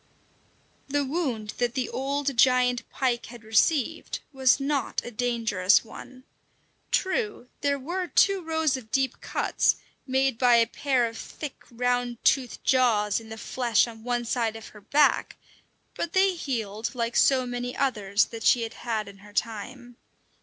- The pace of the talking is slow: No, average, 160 wpm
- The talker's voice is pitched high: Yes, high, 245 Hz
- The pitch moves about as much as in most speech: Yes, average, 3.1 semitones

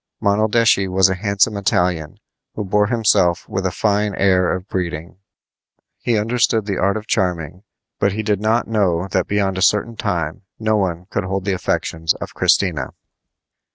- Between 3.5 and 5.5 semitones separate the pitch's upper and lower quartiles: No, average, 2.7 semitones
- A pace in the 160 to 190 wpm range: Yes, average, 165 wpm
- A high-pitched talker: No, low, 100 Hz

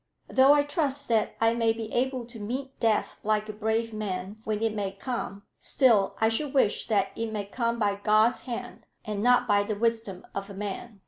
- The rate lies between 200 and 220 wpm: Yes, fast, 205 wpm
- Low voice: No, high, 225 Hz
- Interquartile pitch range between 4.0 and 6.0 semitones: No, average, 2.7 semitones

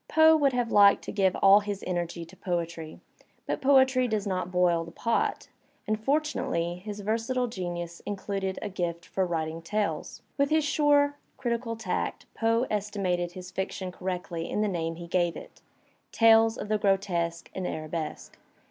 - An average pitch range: Yes, average, 4.6 semitones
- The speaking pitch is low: No, high, 195 Hz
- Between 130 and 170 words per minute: Yes, average, 165 wpm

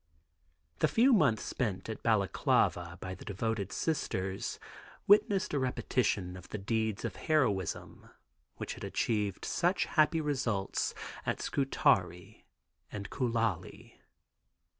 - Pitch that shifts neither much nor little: No, wide, 6.6 semitones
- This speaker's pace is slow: Yes, slow, 115 wpm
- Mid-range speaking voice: No, low, 110 Hz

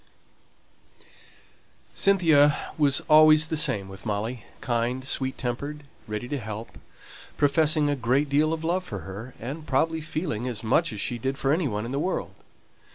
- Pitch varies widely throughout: No, average, 4.8 semitones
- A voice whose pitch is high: No, low, 135 Hz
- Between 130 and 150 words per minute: No, average, 160 wpm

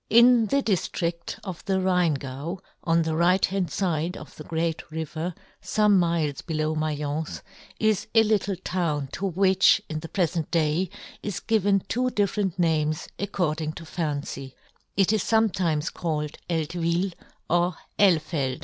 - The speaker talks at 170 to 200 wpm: No, average, 150 wpm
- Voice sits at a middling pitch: Yes, medium, 170 Hz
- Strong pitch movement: No, average, 3.7 semitones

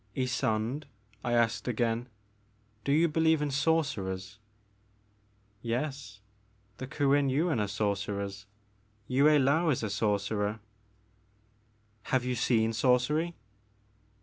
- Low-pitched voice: Yes, low, 120 Hz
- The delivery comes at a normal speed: No, slow, 110 wpm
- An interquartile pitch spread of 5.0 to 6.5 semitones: Yes, average, 5.3 semitones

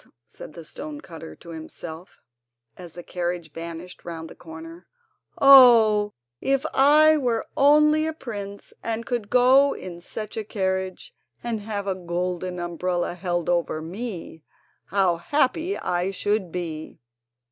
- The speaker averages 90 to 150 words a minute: Yes, slow, 135 wpm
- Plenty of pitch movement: Yes, wide, 5.7 semitones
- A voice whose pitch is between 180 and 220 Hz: Yes, high, 190 Hz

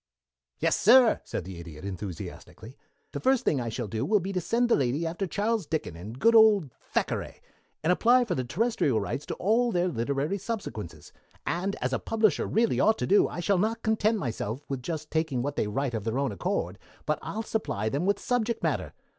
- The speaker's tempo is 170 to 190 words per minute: No, fast, 205 wpm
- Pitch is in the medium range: Yes, medium, 165 Hz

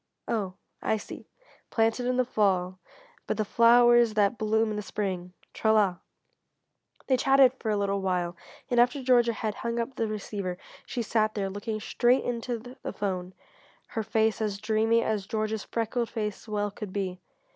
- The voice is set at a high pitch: Yes, high, 220 Hz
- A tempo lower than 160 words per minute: No, average, 170 wpm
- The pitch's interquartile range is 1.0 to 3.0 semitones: Yes, average, 2.7 semitones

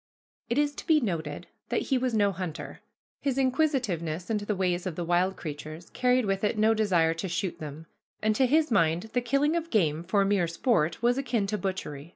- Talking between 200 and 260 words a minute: Yes, fast, 205 wpm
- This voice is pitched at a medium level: No, high, 200 Hz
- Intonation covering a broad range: Yes, wide, 6.5 semitones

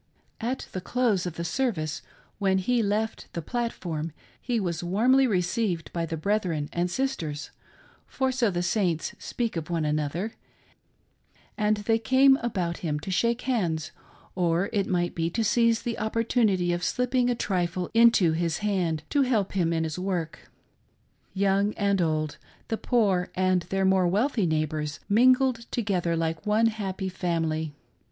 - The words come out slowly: No, average, 160 wpm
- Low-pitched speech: No, high, 190 Hz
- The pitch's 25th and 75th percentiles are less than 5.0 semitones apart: No, average, 5.3 semitones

